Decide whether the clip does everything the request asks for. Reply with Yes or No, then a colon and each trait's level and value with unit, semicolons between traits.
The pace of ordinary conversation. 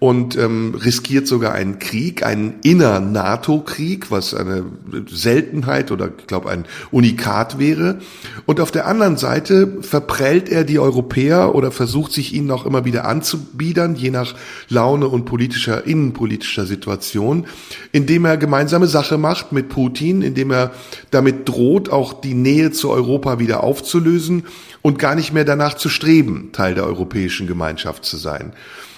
Yes: average, 145 wpm